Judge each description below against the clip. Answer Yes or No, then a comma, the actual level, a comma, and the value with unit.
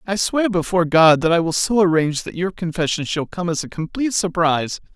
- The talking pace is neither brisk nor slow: No, fast, 220 wpm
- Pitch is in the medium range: Yes, medium, 175 Hz